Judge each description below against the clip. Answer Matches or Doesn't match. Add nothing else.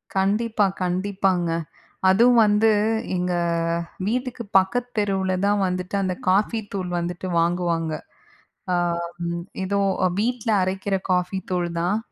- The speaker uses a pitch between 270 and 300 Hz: Doesn't match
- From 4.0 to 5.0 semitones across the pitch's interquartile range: Doesn't match